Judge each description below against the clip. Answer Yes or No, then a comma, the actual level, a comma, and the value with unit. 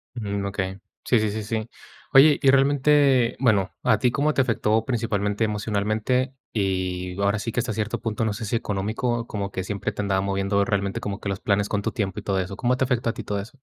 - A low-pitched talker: Yes, low, 105 Hz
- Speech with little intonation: No, average, 3.2 semitones